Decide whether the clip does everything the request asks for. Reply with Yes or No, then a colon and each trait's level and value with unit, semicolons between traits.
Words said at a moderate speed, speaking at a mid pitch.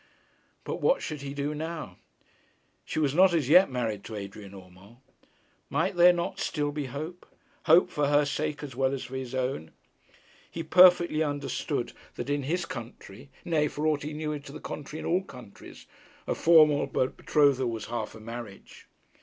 Yes: average, 175 wpm; medium, 145 Hz